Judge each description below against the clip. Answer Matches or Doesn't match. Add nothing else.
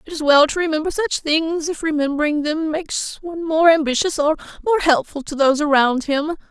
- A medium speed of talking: Matches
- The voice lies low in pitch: Doesn't match